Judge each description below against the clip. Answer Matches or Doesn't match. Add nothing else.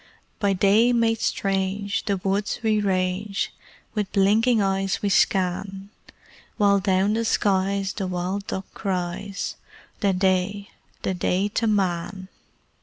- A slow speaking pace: Matches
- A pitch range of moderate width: Doesn't match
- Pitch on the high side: Matches